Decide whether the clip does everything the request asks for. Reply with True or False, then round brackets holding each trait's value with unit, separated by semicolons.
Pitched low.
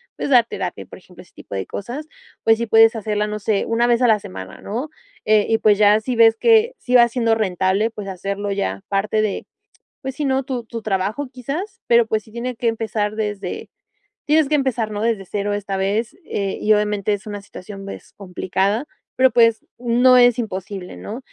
False (220 Hz)